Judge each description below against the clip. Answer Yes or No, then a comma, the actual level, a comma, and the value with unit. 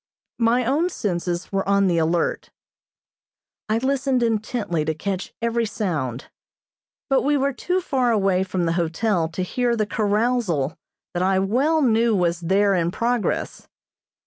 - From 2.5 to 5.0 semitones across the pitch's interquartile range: No, wide, 5.6 semitones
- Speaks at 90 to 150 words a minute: Yes, average, 145 wpm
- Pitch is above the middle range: Yes, high, 205 Hz